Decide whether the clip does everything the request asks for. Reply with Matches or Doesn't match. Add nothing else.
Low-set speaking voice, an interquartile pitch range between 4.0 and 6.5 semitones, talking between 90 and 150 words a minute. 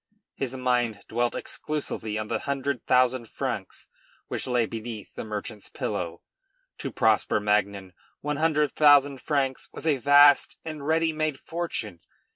Matches